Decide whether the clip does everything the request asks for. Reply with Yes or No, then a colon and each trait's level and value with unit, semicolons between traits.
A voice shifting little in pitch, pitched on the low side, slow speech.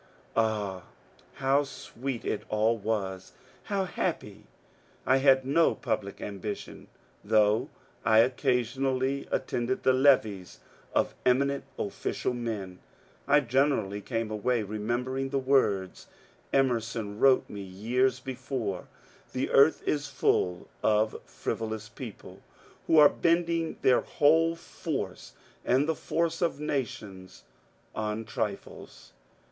No: average, 4.3 semitones; low, 125 Hz; slow, 120 wpm